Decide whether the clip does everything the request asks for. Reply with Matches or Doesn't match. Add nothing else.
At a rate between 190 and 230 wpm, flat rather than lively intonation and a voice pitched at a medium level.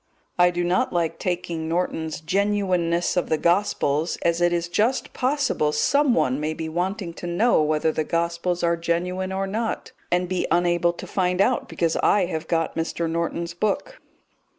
Doesn't match